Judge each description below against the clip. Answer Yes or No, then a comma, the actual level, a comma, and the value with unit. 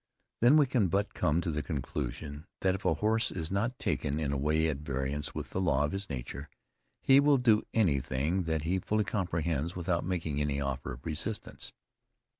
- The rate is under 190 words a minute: No, average, 195 wpm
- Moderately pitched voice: No, very low, 80 Hz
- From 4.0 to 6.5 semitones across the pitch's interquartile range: Yes, average, 5.3 semitones